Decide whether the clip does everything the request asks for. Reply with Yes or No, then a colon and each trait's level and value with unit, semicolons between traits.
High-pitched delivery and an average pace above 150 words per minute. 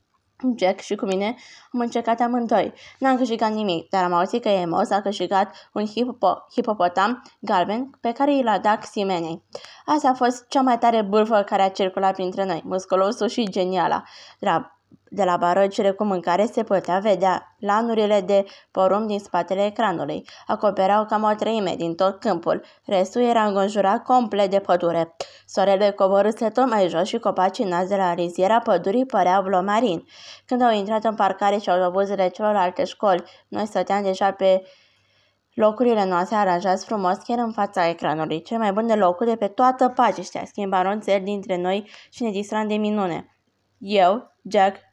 Yes: high, 200 Hz; fast, 170 wpm